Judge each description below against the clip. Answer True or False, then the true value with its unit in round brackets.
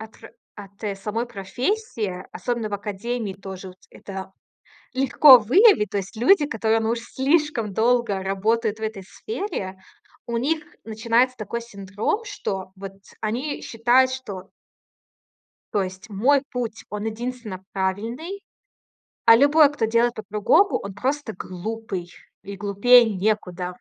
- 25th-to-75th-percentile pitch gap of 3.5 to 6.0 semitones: True (4.0 semitones)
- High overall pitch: True (220 Hz)